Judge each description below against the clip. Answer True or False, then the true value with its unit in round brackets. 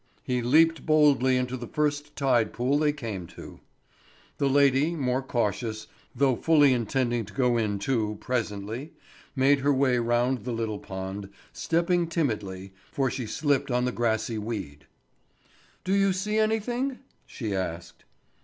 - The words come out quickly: False (145 wpm)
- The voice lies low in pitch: True (125 Hz)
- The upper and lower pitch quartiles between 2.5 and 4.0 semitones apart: False (4.7 semitones)